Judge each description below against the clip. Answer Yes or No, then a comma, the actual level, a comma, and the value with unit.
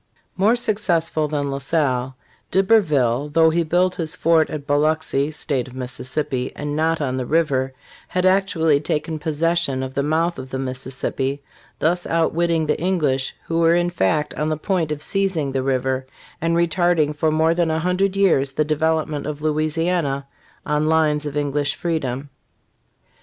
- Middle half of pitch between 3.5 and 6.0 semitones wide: No, average, 3.1 semitones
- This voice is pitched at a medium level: Yes, medium, 155 Hz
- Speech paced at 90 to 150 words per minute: No, average, 165 wpm